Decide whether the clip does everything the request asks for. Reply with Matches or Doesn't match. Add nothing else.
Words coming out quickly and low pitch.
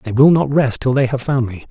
Matches